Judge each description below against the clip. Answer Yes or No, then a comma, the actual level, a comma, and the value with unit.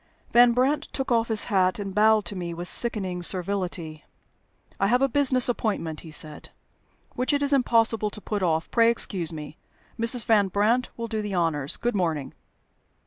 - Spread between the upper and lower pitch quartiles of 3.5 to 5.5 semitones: Yes, average, 5.2 semitones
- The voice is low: No, high, 210 Hz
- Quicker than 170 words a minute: Yes, average, 180 wpm